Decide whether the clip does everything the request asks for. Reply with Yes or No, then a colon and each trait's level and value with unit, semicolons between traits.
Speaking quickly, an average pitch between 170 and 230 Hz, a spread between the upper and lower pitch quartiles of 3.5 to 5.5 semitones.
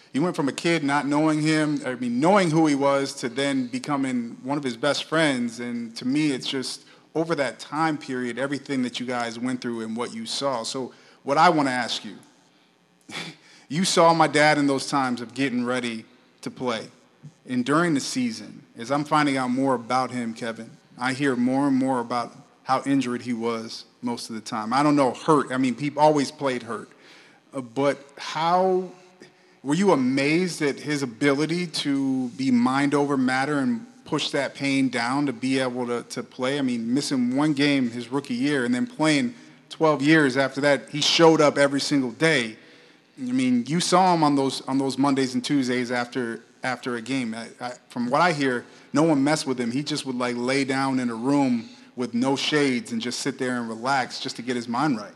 No: fast, 210 wpm; medium, 140 Hz; average, 3.9 semitones